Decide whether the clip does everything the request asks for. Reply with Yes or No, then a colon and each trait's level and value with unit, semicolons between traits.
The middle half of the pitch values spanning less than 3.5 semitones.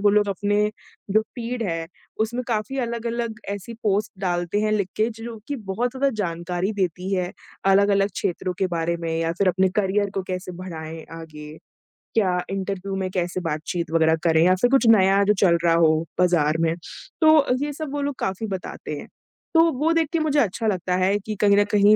No: average, 4.0 semitones